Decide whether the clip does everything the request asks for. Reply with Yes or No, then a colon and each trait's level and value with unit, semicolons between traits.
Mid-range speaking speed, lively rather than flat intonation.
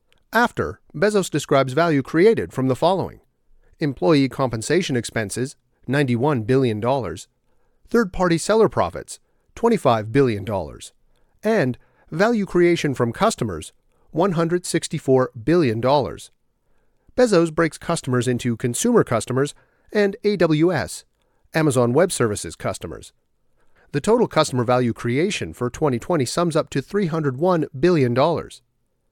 No: slow, 105 wpm; wide, 5.8 semitones